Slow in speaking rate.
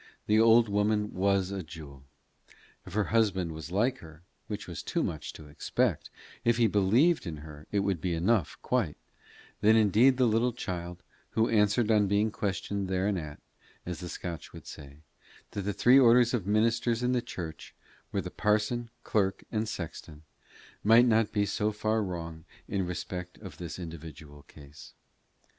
No: average, 165 wpm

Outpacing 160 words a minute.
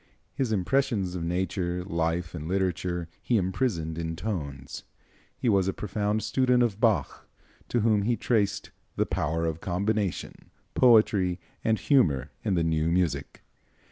No: average, 140 wpm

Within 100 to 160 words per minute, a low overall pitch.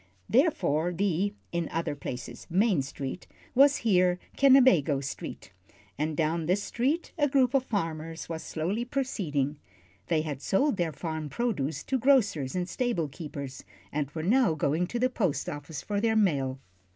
No: average, 155 wpm; medium, 175 Hz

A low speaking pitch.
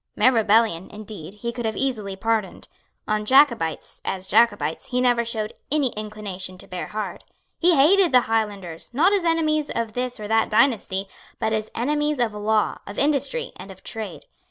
No: high, 225 Hz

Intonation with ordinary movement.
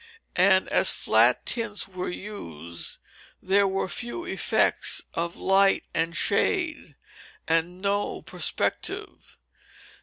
Yes: average, 3.6 semitones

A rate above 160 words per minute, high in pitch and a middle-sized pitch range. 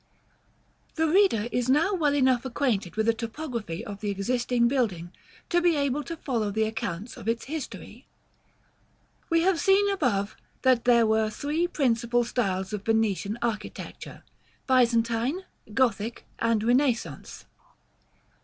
No: average, 140 wpm; high, 235 Hz; average, 4.5 semitones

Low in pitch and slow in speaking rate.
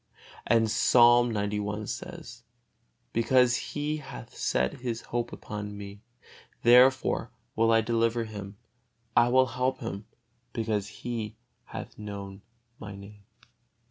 Yes: low, 115 Hz; slow, 115 wpm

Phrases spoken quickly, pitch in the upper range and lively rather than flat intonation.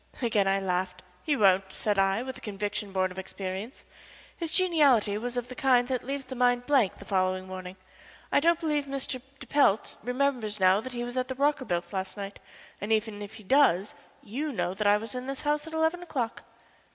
Yes: fast, 210 wpm; high, 225 Hz; wide, 5.8 semitones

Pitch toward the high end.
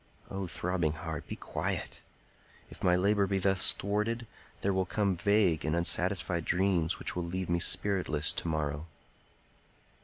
No: very low, 90 Hz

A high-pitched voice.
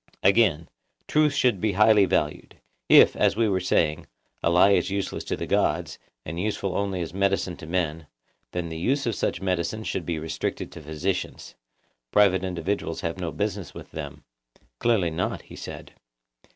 No: very low, 95 Hz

